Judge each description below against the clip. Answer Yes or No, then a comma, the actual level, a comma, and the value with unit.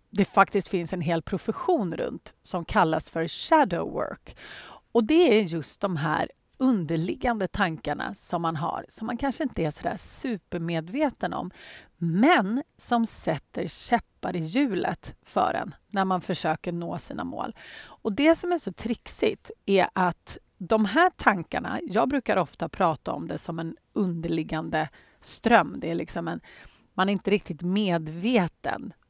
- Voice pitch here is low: No, high, 195 Hz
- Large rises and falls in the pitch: Yes, wide, 6.1 semitones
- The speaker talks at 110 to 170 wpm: Yes, average, 155 wpm